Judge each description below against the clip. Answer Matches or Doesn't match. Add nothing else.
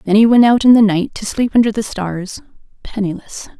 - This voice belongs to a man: Doesn't match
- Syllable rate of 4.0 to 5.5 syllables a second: Matches